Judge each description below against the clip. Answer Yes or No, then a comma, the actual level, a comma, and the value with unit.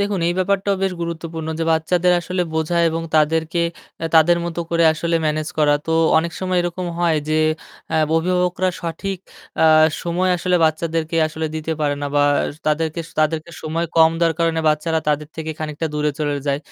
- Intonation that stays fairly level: Yes, narrow, 1.8 semitones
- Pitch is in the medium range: Yes, medium, 165 Hz